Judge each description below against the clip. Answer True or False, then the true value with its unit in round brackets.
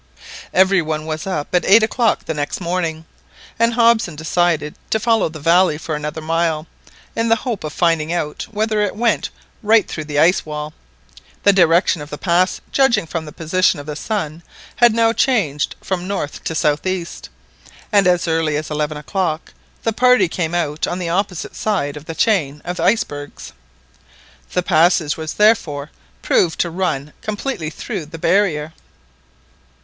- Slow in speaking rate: False (170 wpm)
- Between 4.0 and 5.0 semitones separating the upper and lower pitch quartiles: True (4.7 semitones)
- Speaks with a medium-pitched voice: True (170 Hz)